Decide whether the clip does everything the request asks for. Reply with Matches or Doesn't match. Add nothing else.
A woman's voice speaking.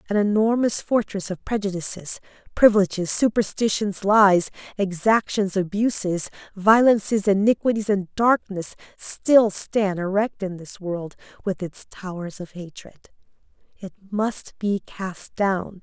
Matches